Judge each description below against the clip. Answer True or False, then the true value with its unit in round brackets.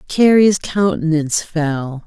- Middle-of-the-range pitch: True (170 Hz)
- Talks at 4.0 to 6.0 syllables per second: False (3.7 syllables/s)